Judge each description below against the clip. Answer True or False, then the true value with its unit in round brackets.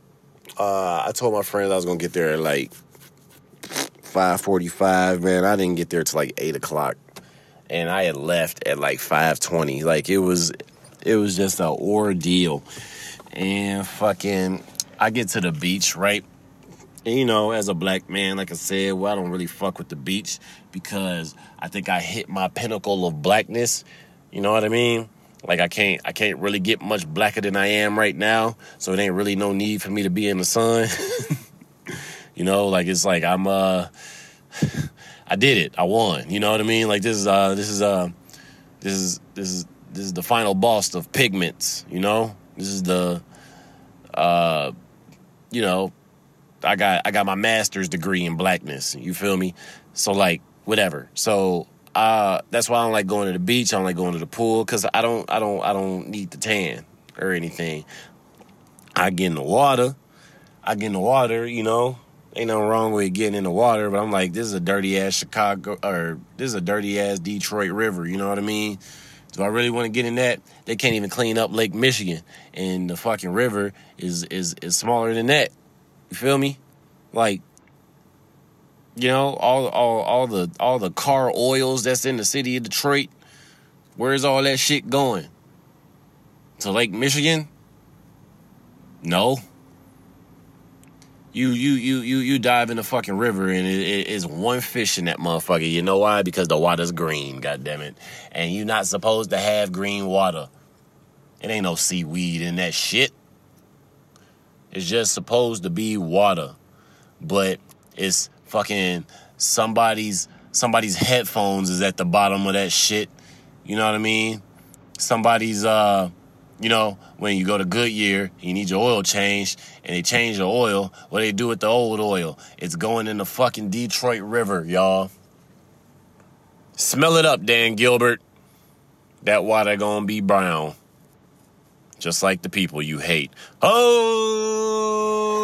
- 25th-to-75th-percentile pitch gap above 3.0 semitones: True (3.8 semitones)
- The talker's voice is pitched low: True (100 Hz)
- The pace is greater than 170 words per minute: True (180 wpm)